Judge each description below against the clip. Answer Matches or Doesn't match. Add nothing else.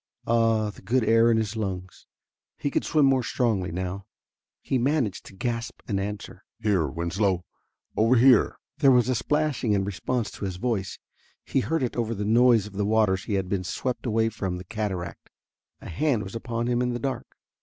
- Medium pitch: Doesn't match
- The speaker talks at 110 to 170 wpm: Doesn't match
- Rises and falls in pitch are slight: Doesn't match